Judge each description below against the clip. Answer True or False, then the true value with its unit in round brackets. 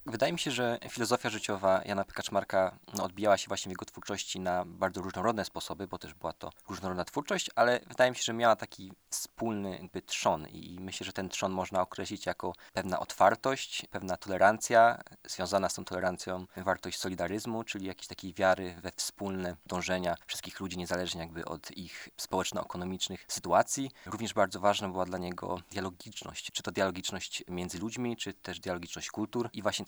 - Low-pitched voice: True (95 Hz)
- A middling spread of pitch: True (3.3 semitones)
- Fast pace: True (170 wpm)